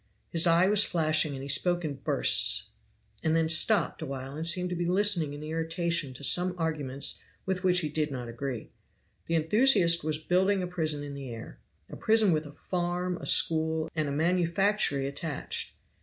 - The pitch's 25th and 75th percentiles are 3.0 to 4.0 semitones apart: Yes, average, 3.5 semitones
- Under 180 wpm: No, average, 185 wpm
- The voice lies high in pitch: No, medium, 160 Hz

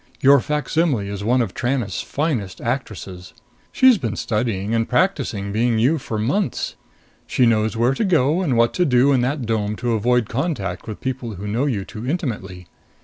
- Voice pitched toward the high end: No, low, 120 Hz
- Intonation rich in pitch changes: No, average, 4.5 semitones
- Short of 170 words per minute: No, average, 180 wpm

